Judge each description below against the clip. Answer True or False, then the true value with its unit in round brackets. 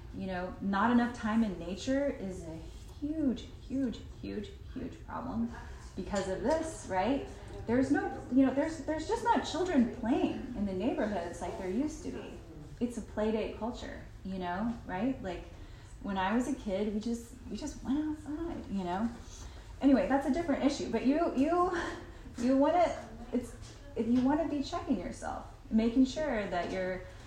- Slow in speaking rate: False (175 wpm)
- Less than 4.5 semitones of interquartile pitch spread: False (5.5 semitones)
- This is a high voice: True (255 Hz)